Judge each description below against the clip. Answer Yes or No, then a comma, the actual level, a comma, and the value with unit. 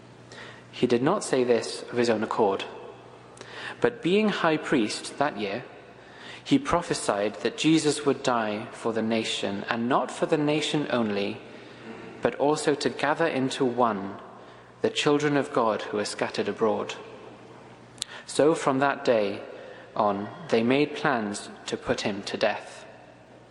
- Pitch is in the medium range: No, low, 130 Hz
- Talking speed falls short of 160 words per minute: Yes, average, 145 wpm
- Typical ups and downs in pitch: No, wide, 6.1 semitones